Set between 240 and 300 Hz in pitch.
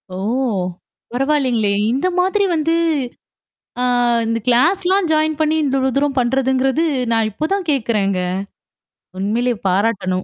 Yes: very high, 265 Hz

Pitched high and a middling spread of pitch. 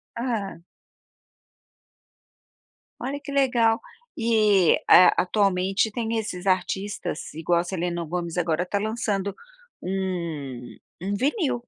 Yes: high, 195 Hz; average, 4.2 semitones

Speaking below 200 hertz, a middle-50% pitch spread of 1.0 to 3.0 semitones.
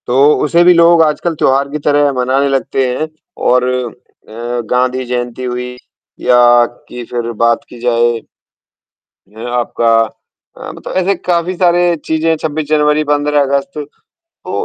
No: medium, 140 Hz; average, 4.3 semitones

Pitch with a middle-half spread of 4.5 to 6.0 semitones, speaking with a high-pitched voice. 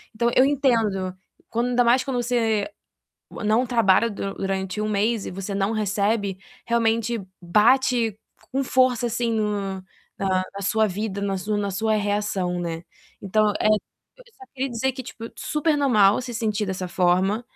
No: average, 3.4 semitones; high, 215 Hz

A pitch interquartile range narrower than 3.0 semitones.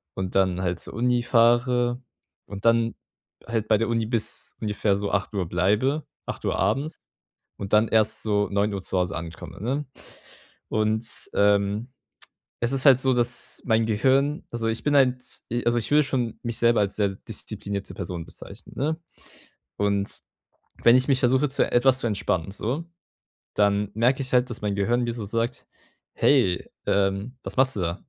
No: average, 3.7 semitones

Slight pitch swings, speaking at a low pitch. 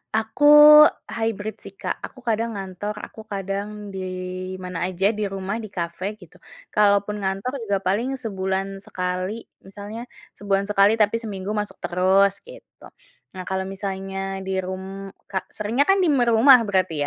No: narrow, 2.1 semitones; high, 200 Hz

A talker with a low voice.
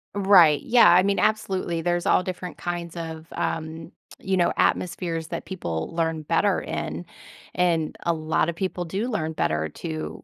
No: medium, 170 Hz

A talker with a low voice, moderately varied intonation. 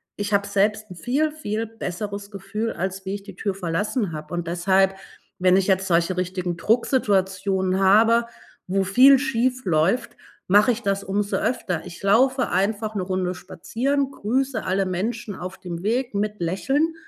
No: high, 200 Hz; average, 3.5 semitones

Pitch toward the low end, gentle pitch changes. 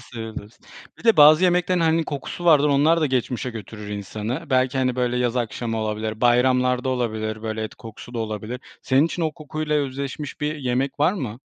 No: low, 125 Hz; average, 4.8 semitones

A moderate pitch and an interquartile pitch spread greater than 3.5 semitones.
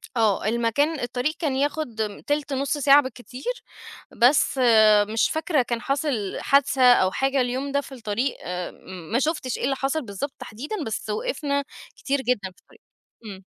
No: very high, 265 Hz; average, 3.9 semitones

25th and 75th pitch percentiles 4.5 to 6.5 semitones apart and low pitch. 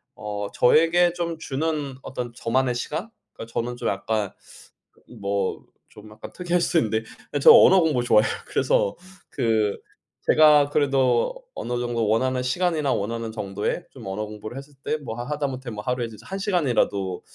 Yes: wide, 5.6 semitones; low, 125 Hz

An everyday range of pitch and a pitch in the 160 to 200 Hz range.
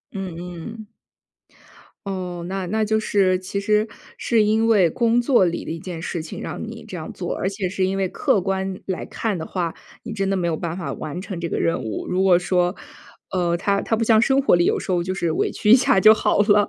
Yes: average, 3.3 semitones; high, 190 Hz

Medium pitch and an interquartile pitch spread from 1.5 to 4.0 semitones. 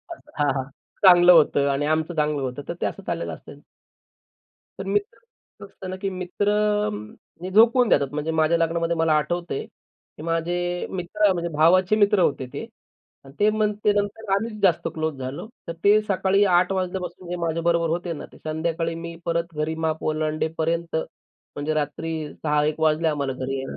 Yes: medium, 170 Hz; average, 3.3 semitones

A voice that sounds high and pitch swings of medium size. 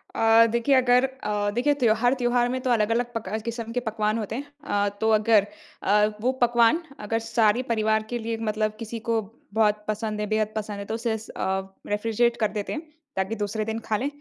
No: high, 225 Hz; narrow, 2.1 semitones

